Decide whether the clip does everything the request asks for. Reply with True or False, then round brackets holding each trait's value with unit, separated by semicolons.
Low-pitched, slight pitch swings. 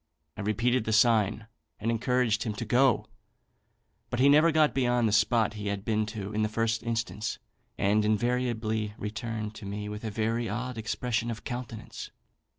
True (110 Hz; 2.3 semitones)